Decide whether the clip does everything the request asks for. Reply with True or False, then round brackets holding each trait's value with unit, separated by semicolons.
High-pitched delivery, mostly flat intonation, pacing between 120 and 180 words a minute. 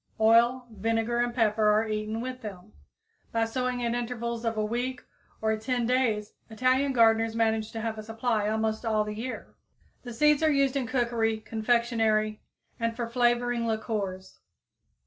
True (230 Hz; 1.9 semitones; 160 wpm)